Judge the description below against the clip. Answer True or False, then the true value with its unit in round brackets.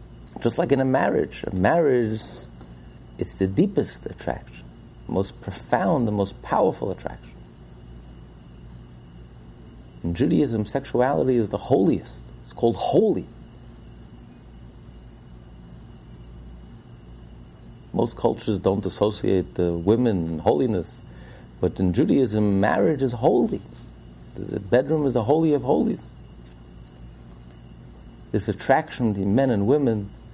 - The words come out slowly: True (105 wpm)